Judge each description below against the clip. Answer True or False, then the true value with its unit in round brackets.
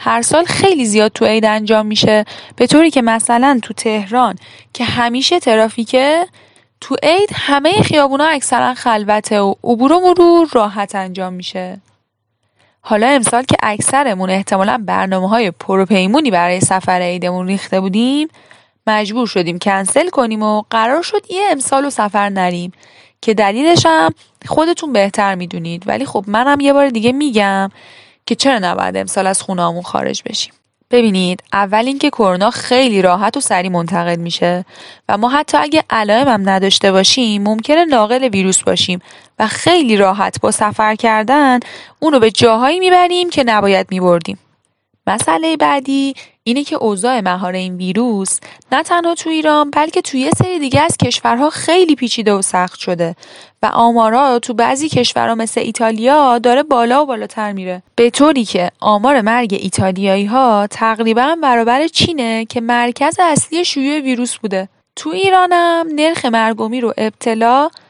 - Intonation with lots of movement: True (6.1 semitones)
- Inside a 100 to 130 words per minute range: False (150 wpm)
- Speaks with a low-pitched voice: False (230 Hz)